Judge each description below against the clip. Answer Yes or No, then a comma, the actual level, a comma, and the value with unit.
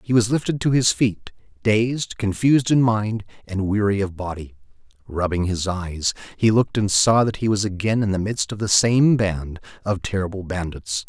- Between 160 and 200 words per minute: Yes, average, 190 wpm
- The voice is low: Yes, low, 105 Hz